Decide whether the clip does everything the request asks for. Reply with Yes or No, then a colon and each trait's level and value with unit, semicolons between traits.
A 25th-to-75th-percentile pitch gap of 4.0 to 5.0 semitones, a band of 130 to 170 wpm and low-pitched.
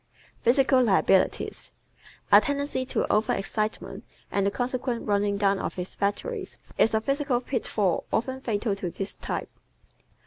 No: average, 4.5 semitones; average, 145 wpm; high, 220 Hz